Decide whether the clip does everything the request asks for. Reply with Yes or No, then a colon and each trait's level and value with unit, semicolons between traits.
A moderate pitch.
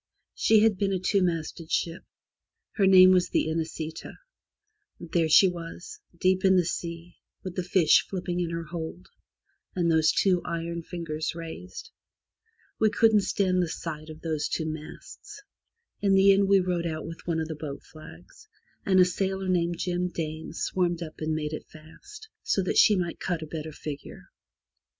Yes: medium, 175 Hz